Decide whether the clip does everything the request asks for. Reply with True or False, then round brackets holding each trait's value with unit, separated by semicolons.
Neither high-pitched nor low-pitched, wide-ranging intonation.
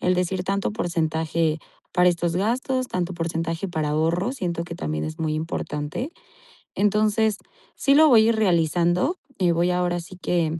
False (175 Hz; 3.4 semitones)